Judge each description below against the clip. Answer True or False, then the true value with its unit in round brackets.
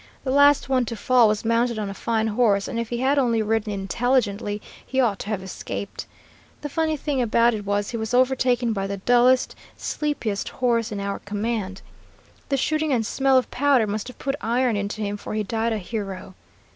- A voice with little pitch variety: False (3.6 semitones)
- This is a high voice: True (230 Hz)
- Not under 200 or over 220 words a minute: True (205 wpm)